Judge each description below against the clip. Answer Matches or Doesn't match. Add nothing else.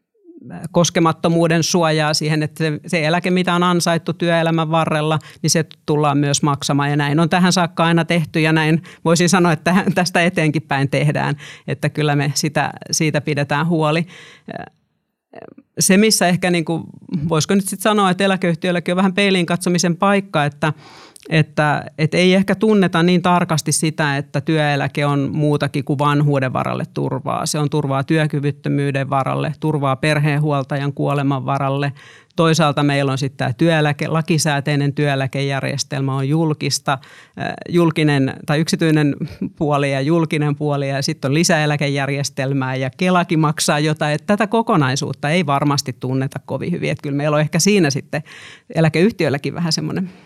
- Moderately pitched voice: Matches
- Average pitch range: Matches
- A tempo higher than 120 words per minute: Matches